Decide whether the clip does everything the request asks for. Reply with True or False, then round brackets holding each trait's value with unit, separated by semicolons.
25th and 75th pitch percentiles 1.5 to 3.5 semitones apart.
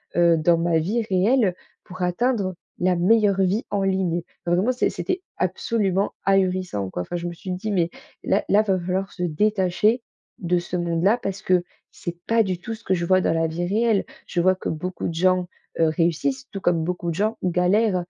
True (2.9 semitones)